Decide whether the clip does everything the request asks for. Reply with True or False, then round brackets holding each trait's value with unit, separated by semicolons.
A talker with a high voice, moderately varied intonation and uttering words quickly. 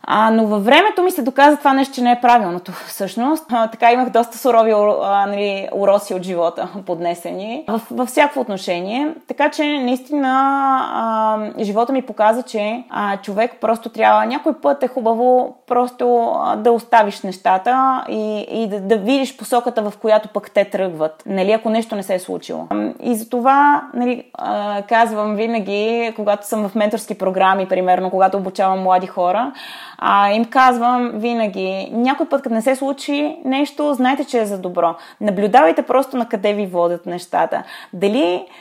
True (225 Hz; 4.2 semitones; 170 wpm)